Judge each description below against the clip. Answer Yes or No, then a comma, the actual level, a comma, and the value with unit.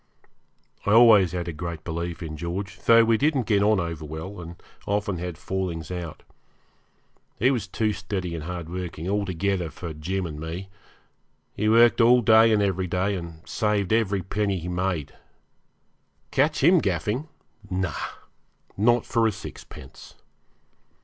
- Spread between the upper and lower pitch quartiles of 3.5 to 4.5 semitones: Yes, average, 3.8 semitones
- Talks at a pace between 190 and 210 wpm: No, average, 150 wpm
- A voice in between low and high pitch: No, very low, 95 Hz